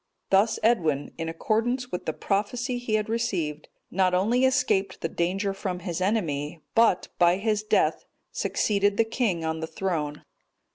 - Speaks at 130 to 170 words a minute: Yes, average, 155 wpm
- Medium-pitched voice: No, high, 195 Hz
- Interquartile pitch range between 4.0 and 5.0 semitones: Yes, average, 4.7 semitones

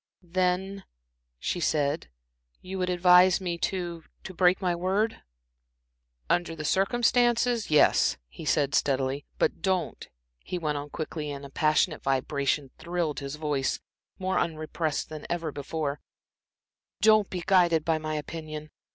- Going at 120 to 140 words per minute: Yes, slow, 135 wpm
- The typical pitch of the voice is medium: Yes, medium, 165 Hz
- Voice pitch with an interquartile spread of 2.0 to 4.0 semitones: Yes, average, 3.6 semitones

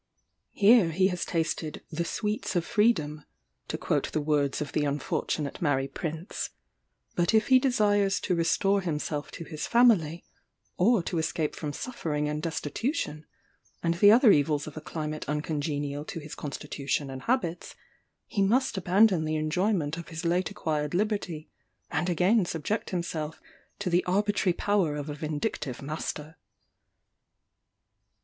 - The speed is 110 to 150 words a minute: Yes, average, 145 wpm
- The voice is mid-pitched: Yes, medium, 165 Hz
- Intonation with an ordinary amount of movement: Yes, average, 4.8 semitones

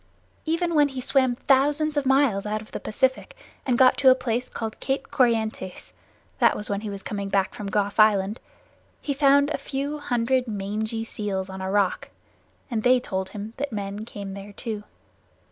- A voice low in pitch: No, high, 225 Hz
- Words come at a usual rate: Yes, average, 185 wpm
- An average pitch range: Yes, average, 4.8 semitones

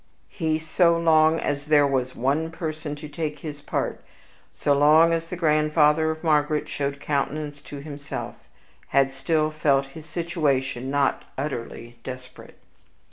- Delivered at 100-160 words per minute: Yes, average, 140 wpm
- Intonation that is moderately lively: No, narrow, 2.1 semitones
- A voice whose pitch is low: No, medium, 150 Hz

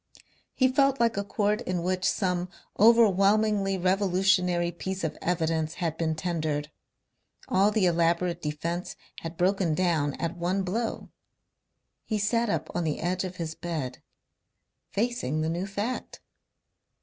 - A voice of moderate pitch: Yes, medium, 180 Hz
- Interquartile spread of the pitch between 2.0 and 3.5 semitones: Yes, average, 3.2 semitones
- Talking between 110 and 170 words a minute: Yes, slow, 135 wpm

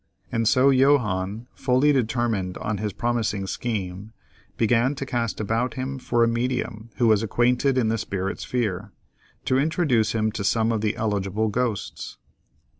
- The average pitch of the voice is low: Yes, low, 115 Hz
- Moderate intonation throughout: Yes, average, 3.0 semitones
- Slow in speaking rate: No, average, 155 wpm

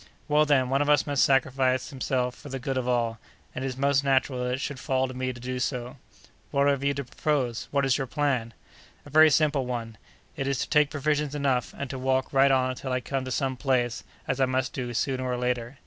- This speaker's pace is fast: Yes, fast, 240 wpm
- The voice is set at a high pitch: No, low, 130 Hz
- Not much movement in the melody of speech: Yes, narrow, 1.9 semitones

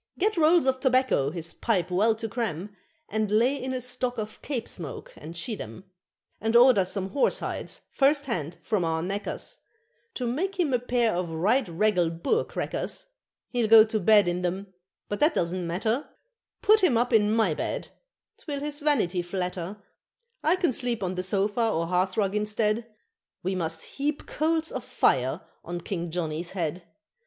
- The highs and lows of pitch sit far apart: Yes, wide, 6.1 semitones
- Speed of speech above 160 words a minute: Yes, average, 170 wpm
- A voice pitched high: Yes, high, 215 Hz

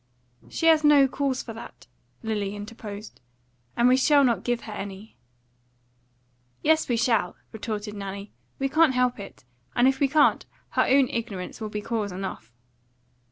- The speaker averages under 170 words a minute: Yes, average, 160 wpm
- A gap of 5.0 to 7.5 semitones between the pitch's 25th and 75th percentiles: No, average, 4.4 semitones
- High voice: Yes, high, 230 Hz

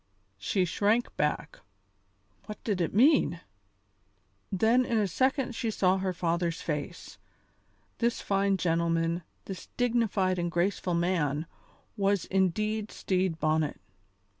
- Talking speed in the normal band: No, slow, 115 wpm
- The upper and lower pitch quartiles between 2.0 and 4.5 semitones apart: Yes, average, 3.9 semitones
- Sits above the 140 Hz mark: Yes, high, 190 Hz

